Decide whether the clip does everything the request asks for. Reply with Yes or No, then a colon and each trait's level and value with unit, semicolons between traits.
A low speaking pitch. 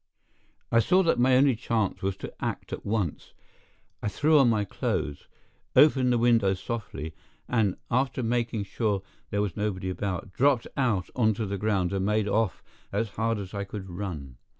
Yes: low, 105 Hz